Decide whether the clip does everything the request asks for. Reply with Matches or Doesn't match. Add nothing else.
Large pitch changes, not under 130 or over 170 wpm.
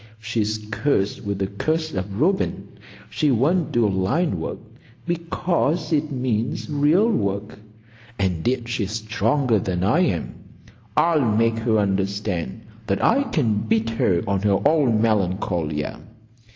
Matches